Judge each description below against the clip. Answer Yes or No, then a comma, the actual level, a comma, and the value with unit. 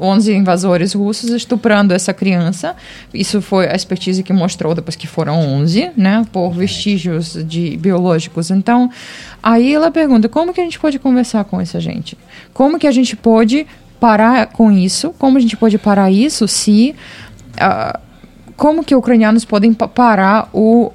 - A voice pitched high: Yes, high, 215 Hz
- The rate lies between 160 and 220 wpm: Yes, average, 165 wpm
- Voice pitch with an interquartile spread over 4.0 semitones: Yes, average, 4.4 semitones